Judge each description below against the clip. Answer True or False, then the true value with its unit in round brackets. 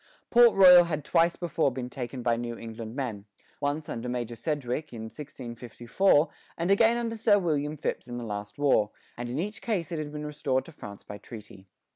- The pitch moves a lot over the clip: True (5.9 semitones)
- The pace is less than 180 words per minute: False (195 wpm)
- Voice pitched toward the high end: False (140 Hz)